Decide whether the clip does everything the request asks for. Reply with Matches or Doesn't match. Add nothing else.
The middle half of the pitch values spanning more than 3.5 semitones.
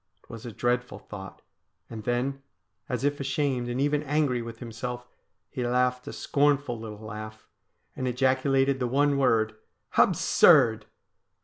Doesn't match